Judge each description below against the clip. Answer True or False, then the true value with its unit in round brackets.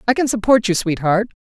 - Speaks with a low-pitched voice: False (210 Hz)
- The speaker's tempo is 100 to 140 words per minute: False (210 wpm)